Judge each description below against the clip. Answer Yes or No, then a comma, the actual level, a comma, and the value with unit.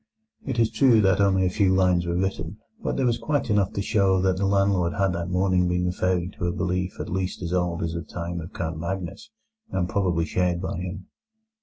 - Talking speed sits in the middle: No, fast, 220 wpm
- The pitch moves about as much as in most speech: No, narrow, 1.9 semitones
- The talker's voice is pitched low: Yes, very low, 90 Hz